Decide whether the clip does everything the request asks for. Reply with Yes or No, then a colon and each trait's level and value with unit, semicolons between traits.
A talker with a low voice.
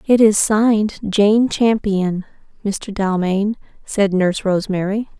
No: high, 205 Hz